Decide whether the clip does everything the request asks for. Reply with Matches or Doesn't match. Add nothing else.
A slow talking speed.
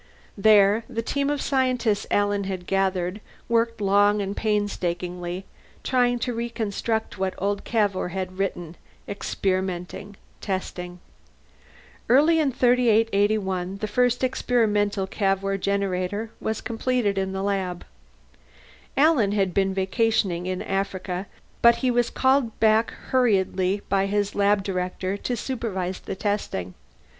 Matches